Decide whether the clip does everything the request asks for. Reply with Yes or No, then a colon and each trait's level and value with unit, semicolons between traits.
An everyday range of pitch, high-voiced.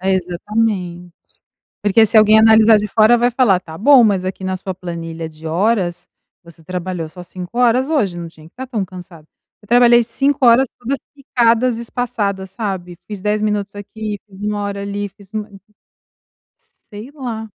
Yes: average, 4.0 semitones; high, 205 Hz